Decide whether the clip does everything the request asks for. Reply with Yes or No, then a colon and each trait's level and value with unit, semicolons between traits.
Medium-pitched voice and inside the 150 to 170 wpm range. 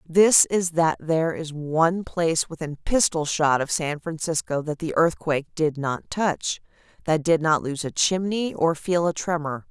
No: medium, 160 Hz; average, 180 wpm